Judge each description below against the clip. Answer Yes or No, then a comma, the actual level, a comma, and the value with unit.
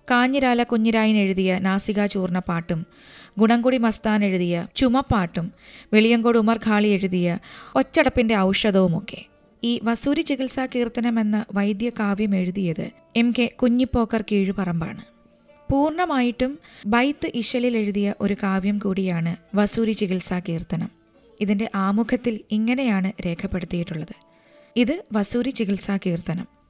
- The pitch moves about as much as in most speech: Yes, average, 3.9 semitones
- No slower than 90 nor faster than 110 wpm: Yes, average, 105 wpm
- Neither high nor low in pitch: No, high, 215 Hz